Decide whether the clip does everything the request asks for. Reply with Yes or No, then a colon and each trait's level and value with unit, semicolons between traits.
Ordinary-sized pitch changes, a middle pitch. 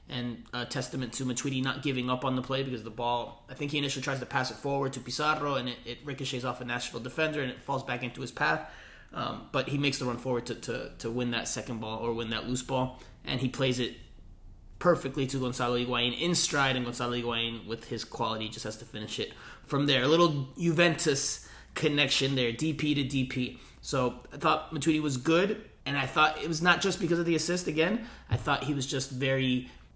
No: average, 3.0 semitones; low, 130 Hz